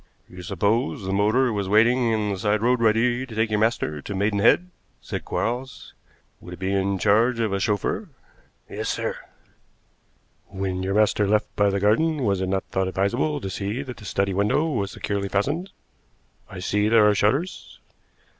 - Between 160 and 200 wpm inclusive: Yes, average, 180 wpm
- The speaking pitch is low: Yes, low, 105 Hz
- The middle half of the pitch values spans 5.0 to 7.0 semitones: No, average, 3.3 semitones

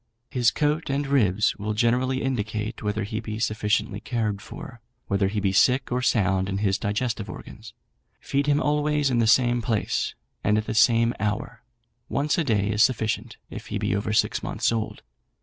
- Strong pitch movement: No, average, 3.5 semitones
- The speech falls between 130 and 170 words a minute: No, average, 185 wpm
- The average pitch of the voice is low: Yes, low, 110 Hz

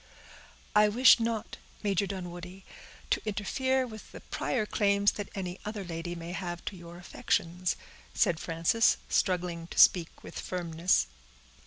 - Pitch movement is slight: No, average, 3.3 semitones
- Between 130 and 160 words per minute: Yes, average, 140 wpm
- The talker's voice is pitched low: No, medium, 185 Hz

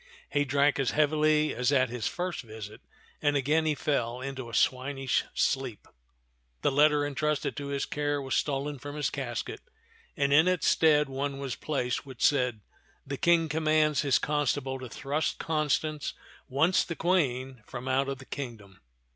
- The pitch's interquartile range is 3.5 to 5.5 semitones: No, narrow, 2.6 semitones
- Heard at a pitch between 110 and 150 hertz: Yes, medium, 140 Hz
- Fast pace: No, average, 165 wpm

